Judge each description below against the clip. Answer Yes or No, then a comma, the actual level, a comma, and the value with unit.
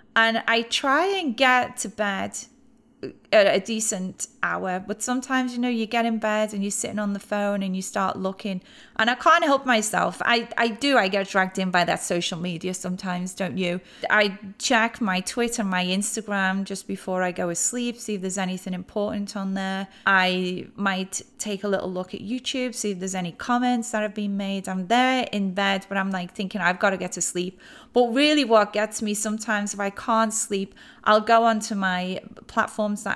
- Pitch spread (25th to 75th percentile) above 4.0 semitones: No, average, 3.4 semitones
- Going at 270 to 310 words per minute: No, fast, 205 wpm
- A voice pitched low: No, high, 205 Hz